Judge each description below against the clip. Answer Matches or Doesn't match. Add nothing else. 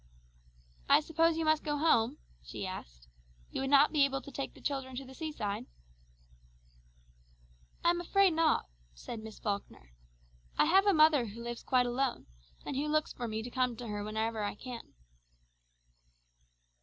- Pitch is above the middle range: Matches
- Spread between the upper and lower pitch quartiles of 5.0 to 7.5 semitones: Matches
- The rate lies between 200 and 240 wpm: Doesn't match